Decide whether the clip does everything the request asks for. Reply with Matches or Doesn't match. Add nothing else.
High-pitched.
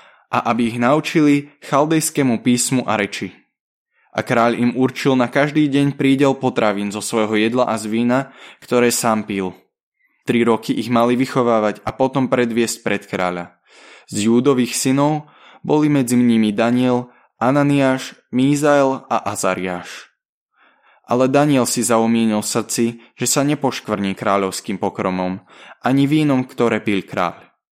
Doesn't match